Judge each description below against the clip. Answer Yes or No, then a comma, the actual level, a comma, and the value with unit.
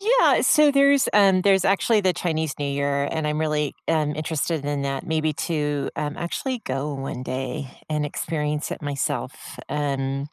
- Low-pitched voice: No, medium, 150 Hz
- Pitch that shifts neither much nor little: Yes, average, 3.6 semitones